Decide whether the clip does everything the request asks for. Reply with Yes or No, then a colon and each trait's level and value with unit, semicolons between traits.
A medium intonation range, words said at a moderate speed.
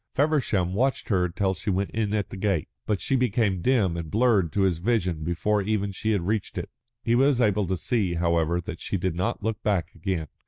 No: average, 4.1 semitones; fast, 220 wpm